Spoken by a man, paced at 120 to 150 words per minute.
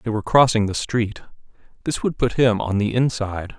No: male; average, 200 wpm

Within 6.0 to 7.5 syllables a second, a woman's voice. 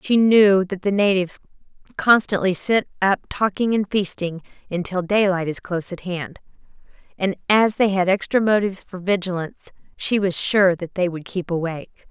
No: 5.1 syllables/s; female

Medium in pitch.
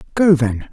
Yes: medium, 145 Hz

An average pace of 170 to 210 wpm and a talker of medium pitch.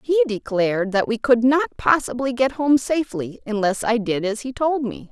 No: average, 200 wpm; high, 240 Hz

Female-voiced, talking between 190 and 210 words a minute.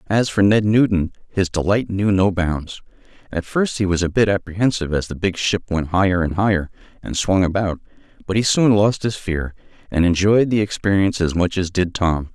No: male; fast, 205 wpm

